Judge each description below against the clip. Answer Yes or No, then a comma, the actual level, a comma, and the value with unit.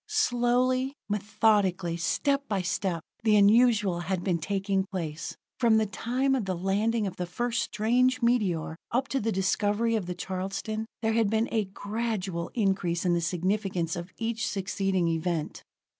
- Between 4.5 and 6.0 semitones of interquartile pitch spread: No, average, 4.0 semitones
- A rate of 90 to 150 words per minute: No, average, 160 wpm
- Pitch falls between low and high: No, high, 205 Hz